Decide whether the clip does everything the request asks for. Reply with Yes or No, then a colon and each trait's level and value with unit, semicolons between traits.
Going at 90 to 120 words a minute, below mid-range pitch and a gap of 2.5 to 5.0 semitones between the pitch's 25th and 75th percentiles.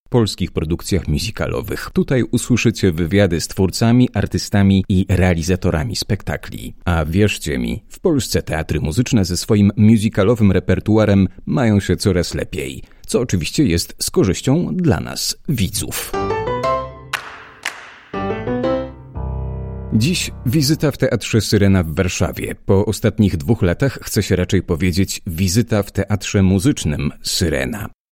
Yes: average, 115 wpm; low, 100 Hz; average, 4.1 semitones